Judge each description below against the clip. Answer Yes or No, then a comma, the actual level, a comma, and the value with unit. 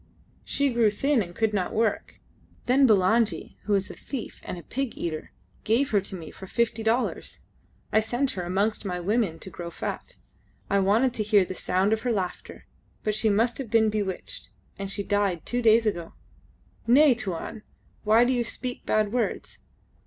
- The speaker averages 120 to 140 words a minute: No, average, 185 wpm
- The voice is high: Yes, high, 215 Hz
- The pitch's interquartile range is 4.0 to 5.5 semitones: No, average, 3.5 semitones